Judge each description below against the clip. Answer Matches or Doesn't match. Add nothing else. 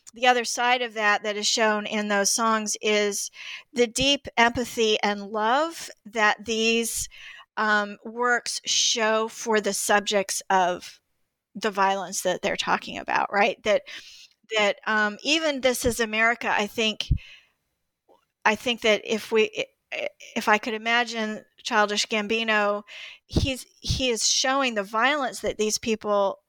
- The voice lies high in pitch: Matches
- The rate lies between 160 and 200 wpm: Doesn't match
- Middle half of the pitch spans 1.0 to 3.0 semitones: Matches